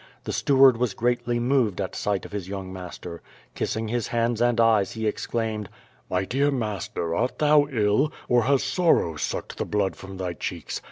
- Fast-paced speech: No, average, 180 wpm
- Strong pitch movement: No, average, 4.2 semitones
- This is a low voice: Yes, low, 110 Hz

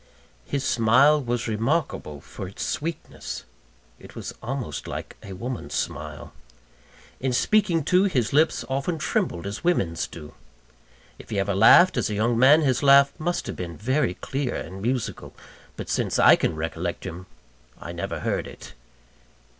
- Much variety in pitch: Yes, wide, 6.9 semitones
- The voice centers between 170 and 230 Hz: No, low, 120 Hz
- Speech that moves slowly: No, average, 155 wpm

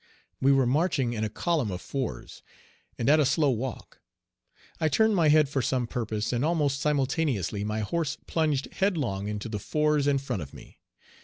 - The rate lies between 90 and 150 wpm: No, average, 180 wpm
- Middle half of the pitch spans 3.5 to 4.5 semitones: No, wide, 5.6 semitones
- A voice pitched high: No, low, 135 Hz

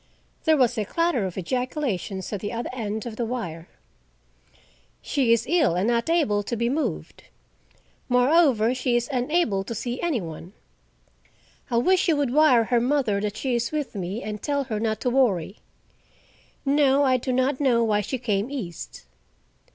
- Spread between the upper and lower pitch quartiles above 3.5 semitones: Yes, average, 4.5 semitones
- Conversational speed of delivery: Yes, average, 175 wpm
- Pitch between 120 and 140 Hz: No, high, 240 Hz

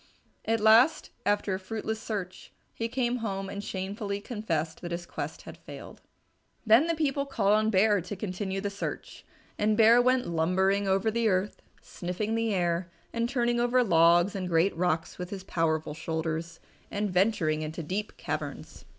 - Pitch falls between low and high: No, high, 200 Hz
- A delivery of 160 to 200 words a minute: Yes, average, 170 wpm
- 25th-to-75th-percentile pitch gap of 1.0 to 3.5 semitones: No, average, 3.9 semitones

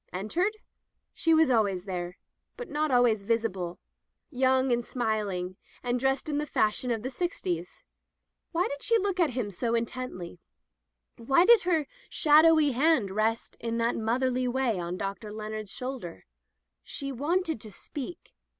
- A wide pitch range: Yes, wide, 5.8 semitones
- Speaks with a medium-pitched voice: No, high, 245 Hz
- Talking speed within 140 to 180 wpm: Yes, average, 160 wpm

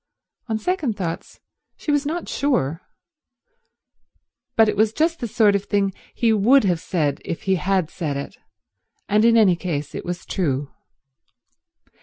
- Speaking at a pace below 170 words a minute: Yes, average, 155 wpm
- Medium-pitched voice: No, high, 200 Hz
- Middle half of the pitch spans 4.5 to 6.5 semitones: Yes, average, 5.0 semitones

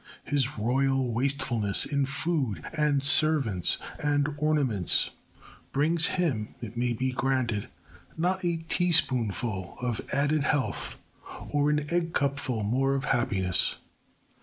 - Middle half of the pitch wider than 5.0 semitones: No, average, 4.0 semitones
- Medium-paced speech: No, slow, 110 wpm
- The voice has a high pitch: No, low, 135 Hz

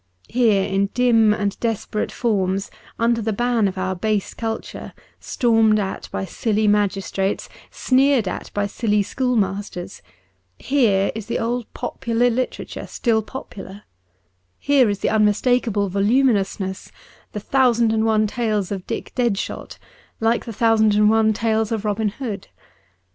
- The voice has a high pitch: Yes, high, 215 Hz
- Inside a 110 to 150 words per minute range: Yes, average, 140 wpm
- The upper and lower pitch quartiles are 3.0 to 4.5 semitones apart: No, narrow, 2.6 semitones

